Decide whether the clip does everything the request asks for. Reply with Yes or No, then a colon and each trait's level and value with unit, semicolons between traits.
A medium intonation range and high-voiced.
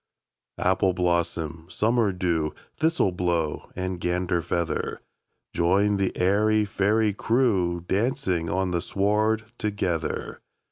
No: average, 3.4 semitones; very low, 95 Hz